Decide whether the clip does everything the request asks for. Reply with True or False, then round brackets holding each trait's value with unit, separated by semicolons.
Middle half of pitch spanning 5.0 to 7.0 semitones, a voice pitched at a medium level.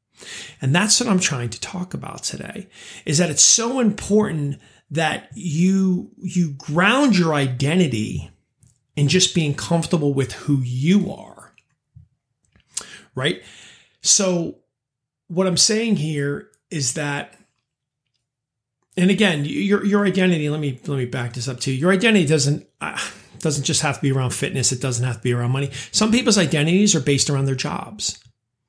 True (5.5 semitones; 150 Hz)